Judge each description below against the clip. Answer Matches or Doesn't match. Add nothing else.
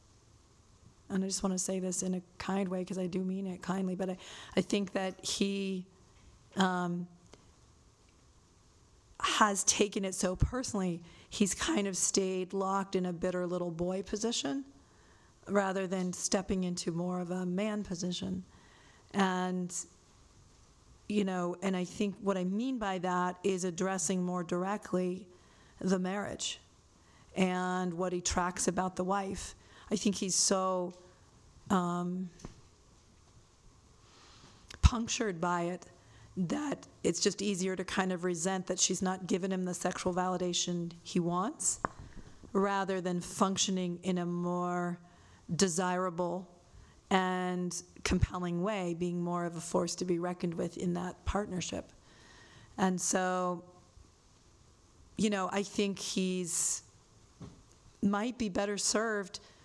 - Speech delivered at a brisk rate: Doesn't match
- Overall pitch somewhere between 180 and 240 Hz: Matches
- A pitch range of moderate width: Doesn't match